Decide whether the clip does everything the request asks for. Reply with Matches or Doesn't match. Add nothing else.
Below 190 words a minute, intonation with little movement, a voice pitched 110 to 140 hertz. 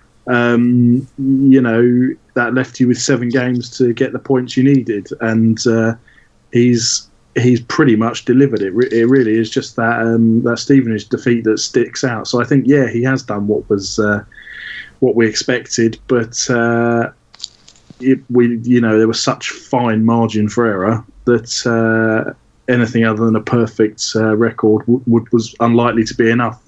Matches